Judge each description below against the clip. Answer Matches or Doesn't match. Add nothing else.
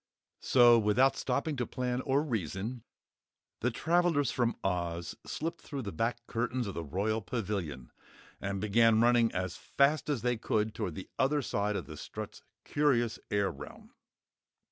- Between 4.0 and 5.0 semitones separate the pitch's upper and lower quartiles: Matches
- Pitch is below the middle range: Matches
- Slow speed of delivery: Doesn't match